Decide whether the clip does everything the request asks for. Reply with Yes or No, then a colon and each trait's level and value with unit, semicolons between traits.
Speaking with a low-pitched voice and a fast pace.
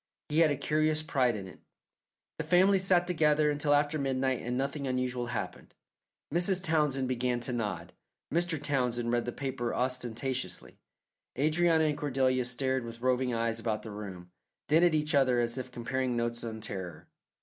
No: low, 130 Hz; average, 170 wpm